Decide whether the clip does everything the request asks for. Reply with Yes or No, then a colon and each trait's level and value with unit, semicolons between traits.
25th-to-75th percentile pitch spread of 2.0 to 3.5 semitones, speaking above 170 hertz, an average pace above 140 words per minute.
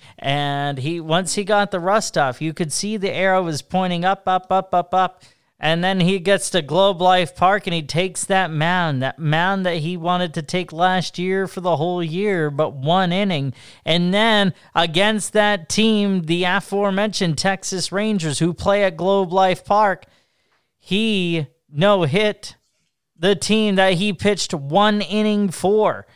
Yes: average, 3.0 semitones; medium, 185 Hz; average, 170 wpm